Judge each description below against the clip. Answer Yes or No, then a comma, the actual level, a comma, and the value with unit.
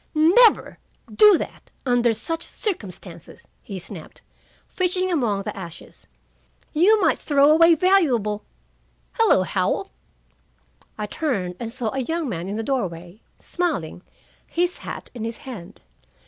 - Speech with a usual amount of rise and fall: No, wide, 8.9 semitones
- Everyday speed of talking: No, slow, 130 wpm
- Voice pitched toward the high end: Yes, very high, 250 Hz